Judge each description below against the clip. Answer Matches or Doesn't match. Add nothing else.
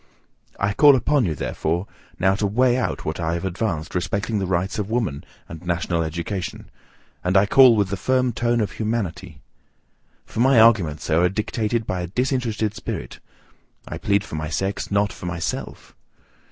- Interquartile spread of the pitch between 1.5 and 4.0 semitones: Doesn't match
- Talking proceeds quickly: Doesn't match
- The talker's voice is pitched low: Matches